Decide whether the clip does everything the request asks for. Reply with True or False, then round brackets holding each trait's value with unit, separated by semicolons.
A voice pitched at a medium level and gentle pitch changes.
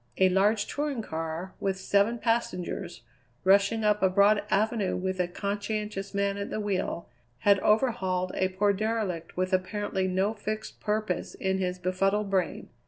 False (200 Hz; 2.2 semitones)